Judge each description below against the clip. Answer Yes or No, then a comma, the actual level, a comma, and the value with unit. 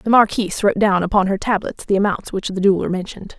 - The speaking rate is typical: No, fast, 230 wpm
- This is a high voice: Yes, high, 200 Hz